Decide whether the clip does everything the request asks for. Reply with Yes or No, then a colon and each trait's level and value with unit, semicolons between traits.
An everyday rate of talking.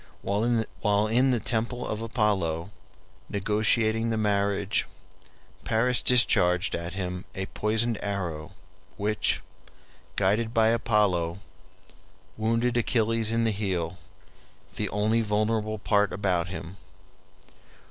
No: slow, 105 wpm